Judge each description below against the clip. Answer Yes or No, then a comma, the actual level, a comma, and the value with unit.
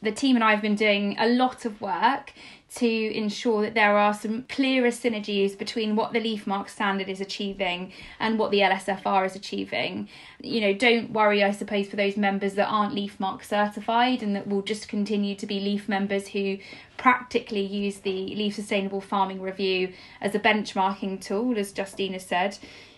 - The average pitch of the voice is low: No, high, 205 Hz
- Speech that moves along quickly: No, average, 180 wpm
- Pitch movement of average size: No, narrow, 1.8 semitones